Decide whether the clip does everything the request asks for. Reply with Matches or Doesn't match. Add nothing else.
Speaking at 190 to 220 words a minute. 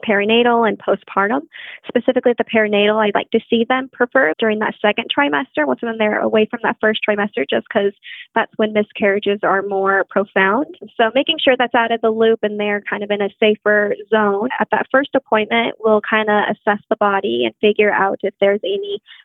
Matches